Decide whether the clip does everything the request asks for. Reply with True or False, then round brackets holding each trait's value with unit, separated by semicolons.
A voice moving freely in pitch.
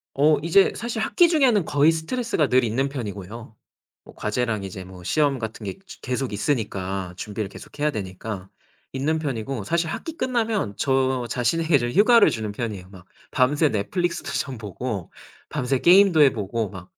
True (7.2 semitones)